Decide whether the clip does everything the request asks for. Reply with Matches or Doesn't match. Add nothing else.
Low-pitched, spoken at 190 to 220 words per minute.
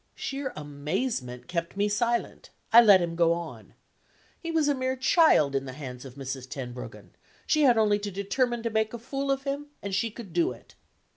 Doesn't match